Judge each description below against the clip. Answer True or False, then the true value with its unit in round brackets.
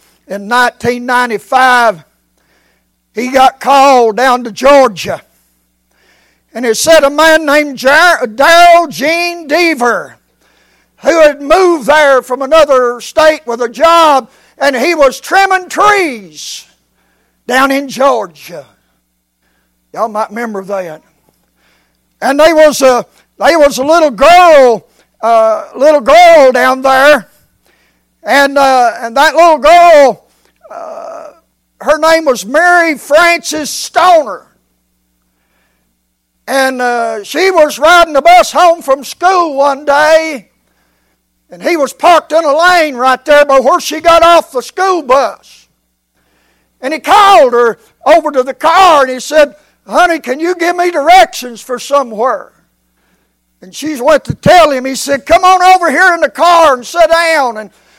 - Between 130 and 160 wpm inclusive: True (135 wpm)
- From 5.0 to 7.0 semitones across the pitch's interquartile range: True (5.3 semitones)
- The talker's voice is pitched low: False (280 Hz)